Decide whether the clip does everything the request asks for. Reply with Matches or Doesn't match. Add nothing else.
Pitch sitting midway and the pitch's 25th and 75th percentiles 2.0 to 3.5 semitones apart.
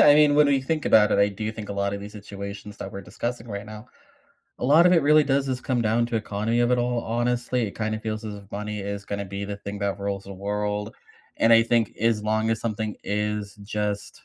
Doesn't match